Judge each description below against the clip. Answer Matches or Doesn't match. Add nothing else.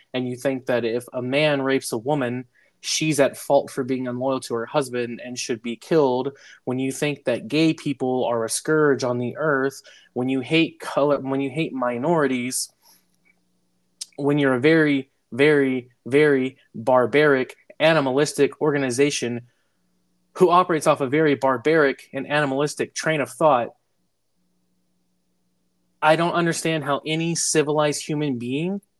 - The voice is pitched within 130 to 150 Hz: Matches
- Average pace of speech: Matches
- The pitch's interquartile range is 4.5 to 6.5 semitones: Doesn't match